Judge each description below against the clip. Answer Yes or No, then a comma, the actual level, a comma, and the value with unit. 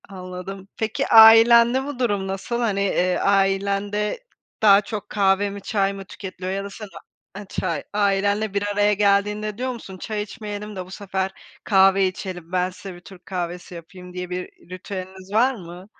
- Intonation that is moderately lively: No, narrow, 1.9 semitones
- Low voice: No, high, 195 Hz